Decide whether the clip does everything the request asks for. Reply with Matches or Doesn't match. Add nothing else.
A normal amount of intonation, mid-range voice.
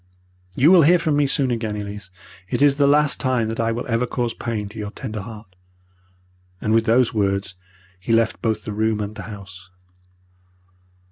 Doesn't match